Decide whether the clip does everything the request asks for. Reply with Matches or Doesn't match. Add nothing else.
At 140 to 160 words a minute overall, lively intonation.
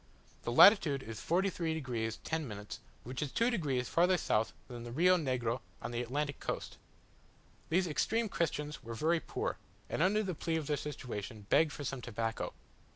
Doesn't match